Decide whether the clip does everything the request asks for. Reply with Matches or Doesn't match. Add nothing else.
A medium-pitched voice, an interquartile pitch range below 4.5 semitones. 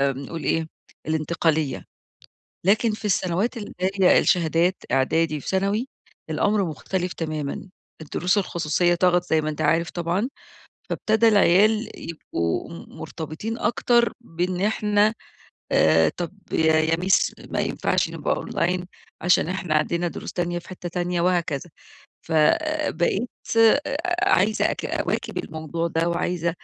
Matches